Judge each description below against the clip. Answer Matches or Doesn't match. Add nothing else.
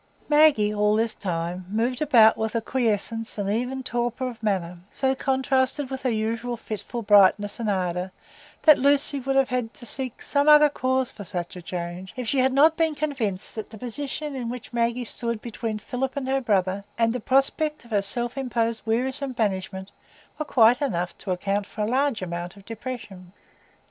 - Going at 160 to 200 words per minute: Matches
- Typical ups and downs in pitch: Matches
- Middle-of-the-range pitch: Doesn't match